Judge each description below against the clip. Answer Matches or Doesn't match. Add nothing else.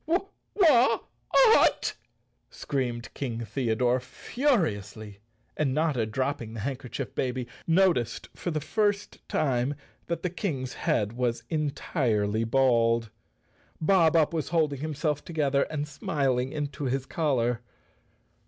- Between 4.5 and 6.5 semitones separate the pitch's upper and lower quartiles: Matches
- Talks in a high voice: Doesn't match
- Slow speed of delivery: Matches